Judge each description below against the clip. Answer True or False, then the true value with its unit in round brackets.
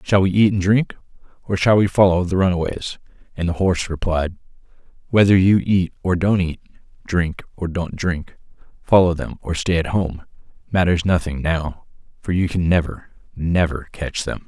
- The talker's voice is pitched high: False (90 Hz)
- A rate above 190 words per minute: False (170 wpm)